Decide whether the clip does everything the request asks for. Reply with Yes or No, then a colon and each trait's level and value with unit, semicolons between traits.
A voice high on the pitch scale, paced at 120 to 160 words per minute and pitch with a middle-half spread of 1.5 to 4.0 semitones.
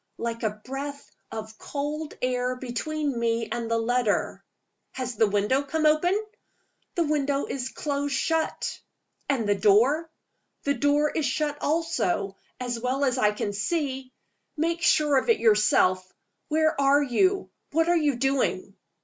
No: very high, 275 Hz; average, 150 wpm; average, 4.5 semitones